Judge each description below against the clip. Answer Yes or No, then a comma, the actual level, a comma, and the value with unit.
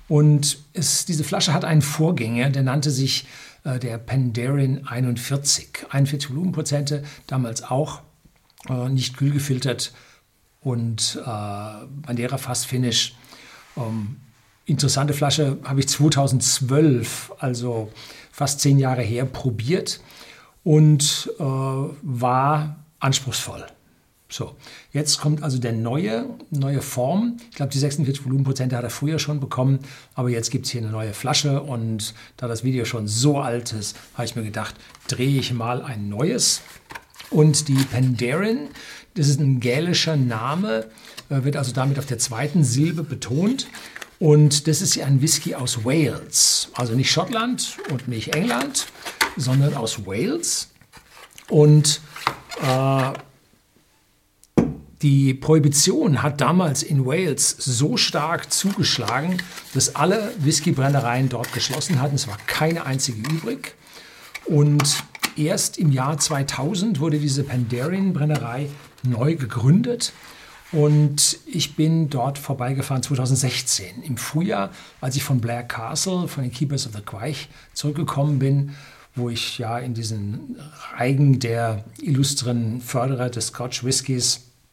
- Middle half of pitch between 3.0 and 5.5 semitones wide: Yes, average, 3.4 semitones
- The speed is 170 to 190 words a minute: No, average, 130 wpm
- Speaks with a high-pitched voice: No, low, 135 Hz